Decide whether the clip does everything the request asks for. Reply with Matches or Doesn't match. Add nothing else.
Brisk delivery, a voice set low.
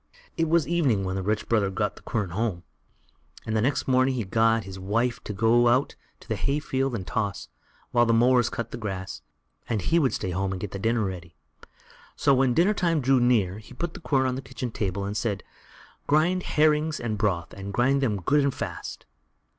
Matches